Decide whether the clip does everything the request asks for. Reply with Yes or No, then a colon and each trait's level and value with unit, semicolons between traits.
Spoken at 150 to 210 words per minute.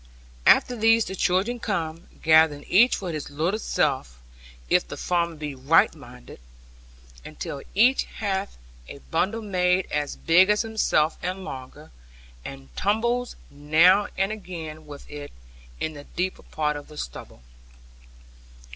No: average, 140 wpm